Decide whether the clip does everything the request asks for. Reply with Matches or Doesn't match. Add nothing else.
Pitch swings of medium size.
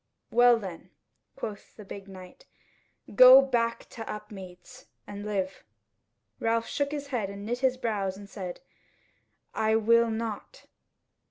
Matches